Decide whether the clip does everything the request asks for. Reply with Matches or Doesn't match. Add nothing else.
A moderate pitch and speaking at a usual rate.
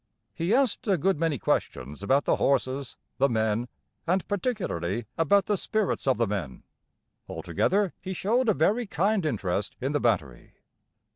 Matches